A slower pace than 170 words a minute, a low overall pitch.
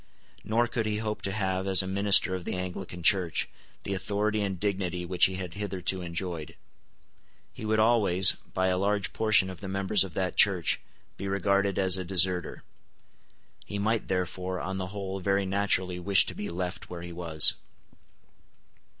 No: average, 175 wpm; very low, 95 Hz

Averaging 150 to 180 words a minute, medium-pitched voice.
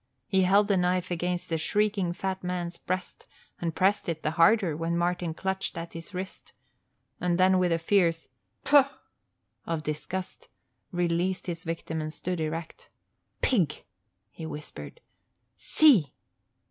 No: slow, 135 wpm; medium, 180 Hz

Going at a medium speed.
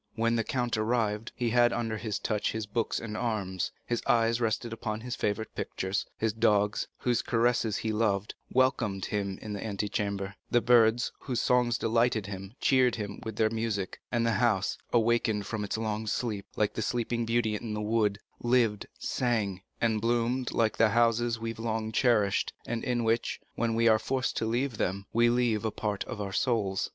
Yes: average, 190 wpm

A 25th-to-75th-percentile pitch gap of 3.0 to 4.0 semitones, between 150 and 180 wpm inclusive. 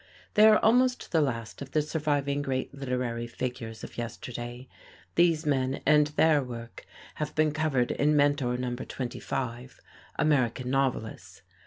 No: average, 3.5 semitones; average, 140 wpm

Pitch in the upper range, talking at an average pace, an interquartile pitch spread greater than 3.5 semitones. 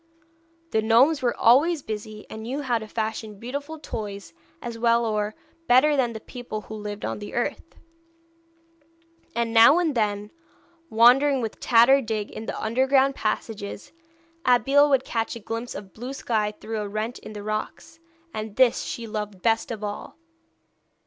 No: high, 230 Hz; average, 165 wpm; average, 3.1 semitones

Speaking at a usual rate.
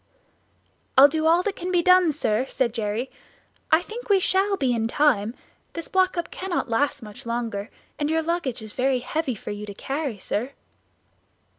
Yes: average, 180 wpm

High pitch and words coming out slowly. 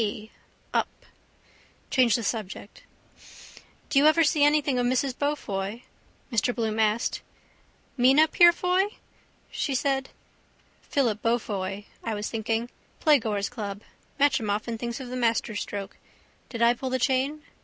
Yes: high, 240 Hz; slow, 130 wpm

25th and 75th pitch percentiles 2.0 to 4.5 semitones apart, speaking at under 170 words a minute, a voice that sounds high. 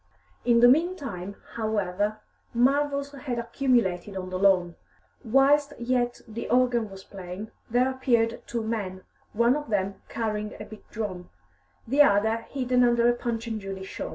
Yes: average, 3.8 semitones; average, 155 wpm; high, 230 Hz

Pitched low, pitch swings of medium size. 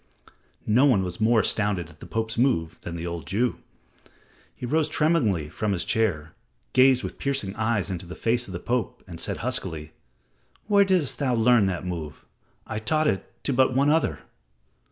No: low, 110 Hz; wide, 6.5 semitones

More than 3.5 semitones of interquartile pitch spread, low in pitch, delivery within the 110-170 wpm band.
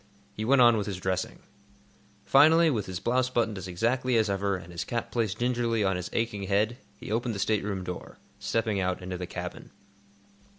No: average, 4.0 semitones; low, 105 Hz; average, 195 wpm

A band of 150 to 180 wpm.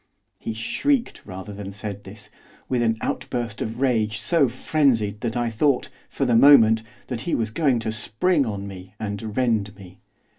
Yes: average, 175 wpm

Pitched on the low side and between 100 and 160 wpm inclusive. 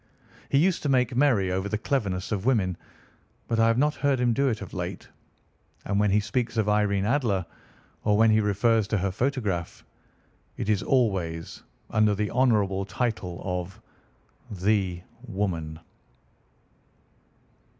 Yes: low, 105 Hz; average, 150 wpm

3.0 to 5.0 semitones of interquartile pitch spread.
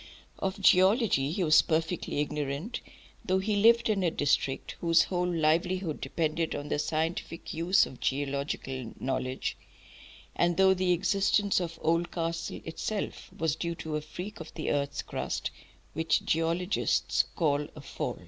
Yes: average, 3.6 semitones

